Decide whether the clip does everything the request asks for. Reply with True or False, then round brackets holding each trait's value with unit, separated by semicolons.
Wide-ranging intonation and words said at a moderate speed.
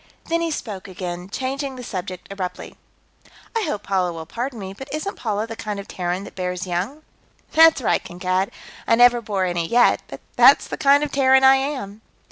True (6.4 semitones; 195 wpm)